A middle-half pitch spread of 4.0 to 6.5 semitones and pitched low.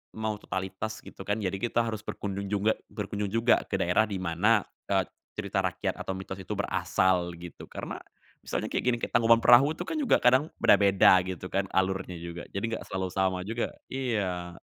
No: average, 3.4 semitones; low, 100 Hz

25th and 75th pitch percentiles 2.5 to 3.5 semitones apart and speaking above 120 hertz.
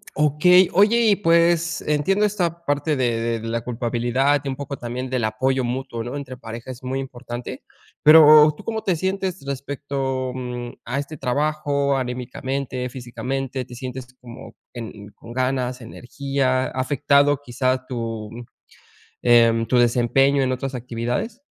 Yes: average, 2.9 semitones; low, 130 Hz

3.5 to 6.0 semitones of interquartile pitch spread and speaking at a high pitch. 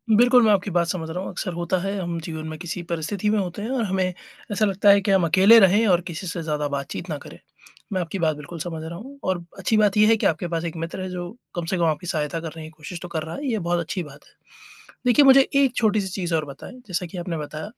No: average, 3.8 semitones; medium, 180 Hz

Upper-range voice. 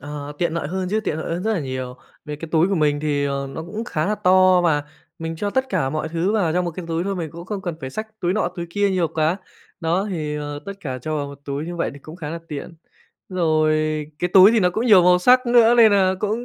No: medium, 170 Hz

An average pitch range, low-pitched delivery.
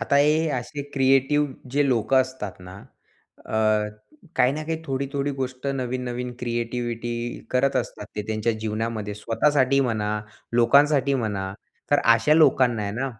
Yes: average, 3.6 semitones; low, 125 Hz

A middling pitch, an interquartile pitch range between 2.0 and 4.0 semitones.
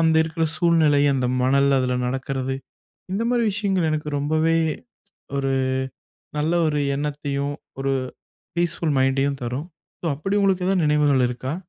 Yes: medium, 150 Hz; average, 3.3 semitones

